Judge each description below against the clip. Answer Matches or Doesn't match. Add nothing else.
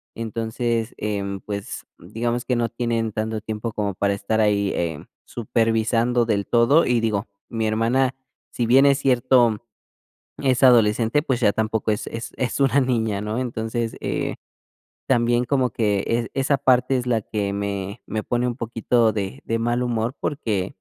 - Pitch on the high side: Doesn't match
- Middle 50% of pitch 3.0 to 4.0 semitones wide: Doesn't match